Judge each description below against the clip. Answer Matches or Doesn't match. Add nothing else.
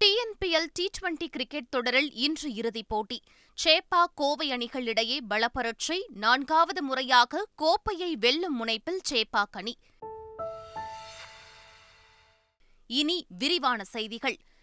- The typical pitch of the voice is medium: Doesn't match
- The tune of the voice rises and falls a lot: Matches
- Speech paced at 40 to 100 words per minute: Matches